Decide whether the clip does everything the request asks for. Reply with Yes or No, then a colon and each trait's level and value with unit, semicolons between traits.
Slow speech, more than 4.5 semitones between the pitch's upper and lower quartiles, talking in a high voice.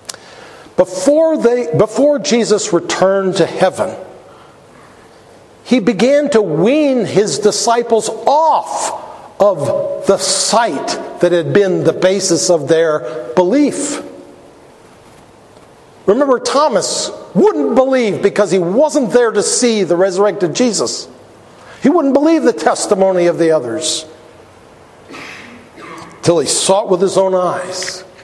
Yes: slow, 115 wpm; wide, 5.4 semitones; high, 200 Hz